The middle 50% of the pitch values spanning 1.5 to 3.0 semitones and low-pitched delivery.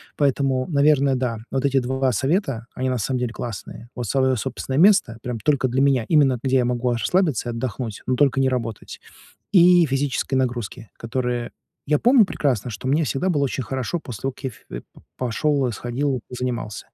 Yes: narrow, 2.5 semitones; low, 130 Hz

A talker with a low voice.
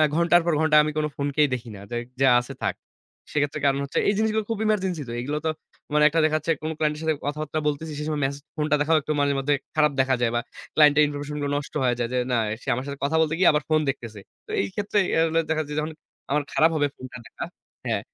No: medium, 150 Hz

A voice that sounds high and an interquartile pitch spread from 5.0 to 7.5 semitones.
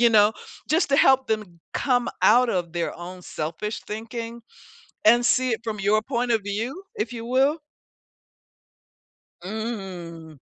No: high, 220 Hz; average, 4.0 semitones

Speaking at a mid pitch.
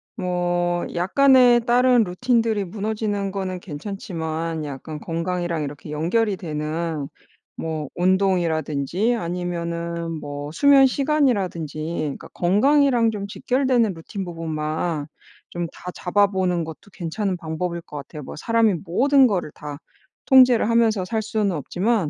Yes: medium, 180 Hz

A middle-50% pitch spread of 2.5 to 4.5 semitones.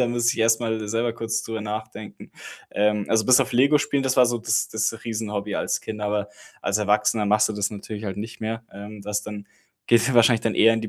No: narrow, 1.7 semitones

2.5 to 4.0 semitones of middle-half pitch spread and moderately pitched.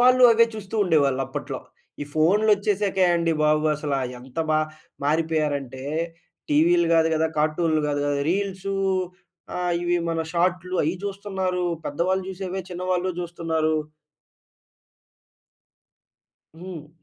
Yes: average, 3.5 semitones; medium, 175 Hz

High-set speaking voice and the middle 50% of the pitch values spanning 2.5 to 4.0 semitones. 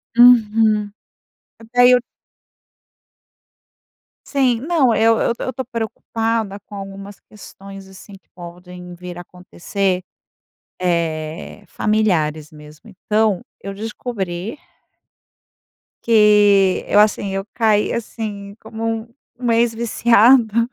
Yes: high, 210 Hz; average, 3.3 semitones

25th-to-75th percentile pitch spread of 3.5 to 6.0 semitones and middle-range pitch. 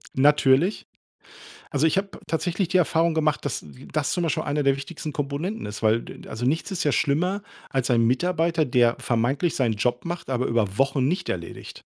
Yes: average, 5.3 semitones; medium, 145 Hz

